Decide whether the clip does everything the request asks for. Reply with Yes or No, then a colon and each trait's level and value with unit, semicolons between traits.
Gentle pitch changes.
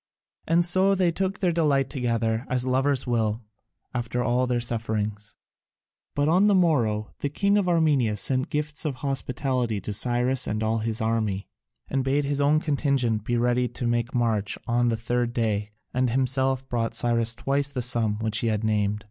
No: average, 3.8 semitones